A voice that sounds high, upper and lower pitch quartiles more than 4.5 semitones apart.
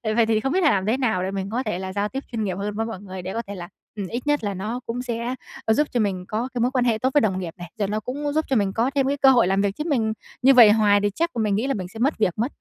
No: high, 220 Hz; average, 4.2 semitones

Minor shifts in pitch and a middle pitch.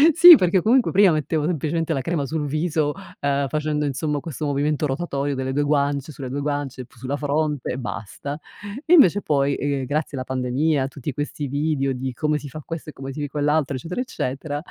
Yes: narrow, 2.3 semitones; medium, 145 Hz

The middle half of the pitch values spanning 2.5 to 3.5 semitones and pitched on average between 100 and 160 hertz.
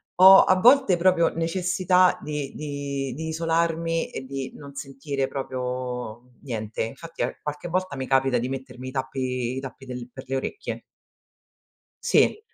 No: average, 4.3 semitones; medium, 140 Hz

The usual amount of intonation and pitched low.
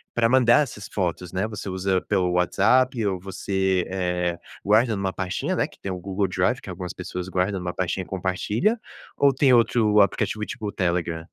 Yes: average, 3.2 semitones; very low, 95 Hz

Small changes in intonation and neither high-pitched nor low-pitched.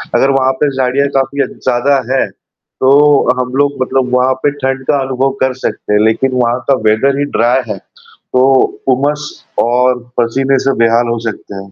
No: narrow, 1.9 semitones; low, 130 Hz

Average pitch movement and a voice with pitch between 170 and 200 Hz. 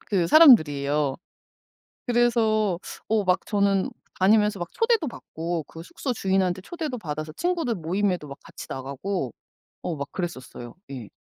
No: wide, 6.2 semitones; medium, 185 Hz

